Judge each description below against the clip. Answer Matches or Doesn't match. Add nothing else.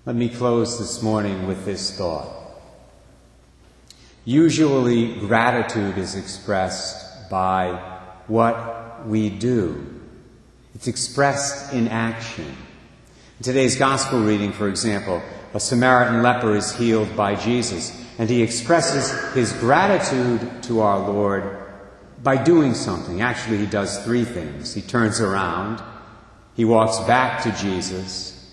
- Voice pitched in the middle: Doesn't match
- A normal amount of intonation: Matches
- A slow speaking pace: Matches